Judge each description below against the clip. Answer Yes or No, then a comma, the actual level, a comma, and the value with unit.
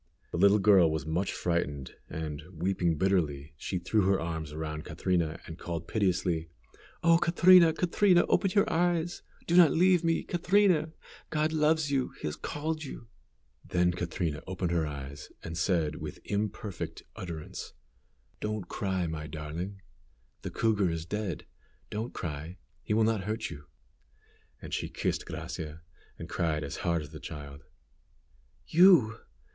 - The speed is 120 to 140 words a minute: No, average, 150 wpm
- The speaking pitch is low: Yes, very low, 90 Hz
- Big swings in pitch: Yes, wide, 8.5 semitones